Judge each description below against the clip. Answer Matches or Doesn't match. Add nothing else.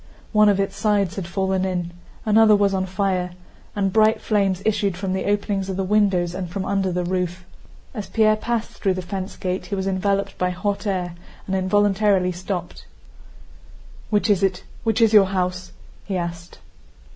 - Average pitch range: Doesn't match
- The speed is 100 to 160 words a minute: Doesn't match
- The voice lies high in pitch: Matches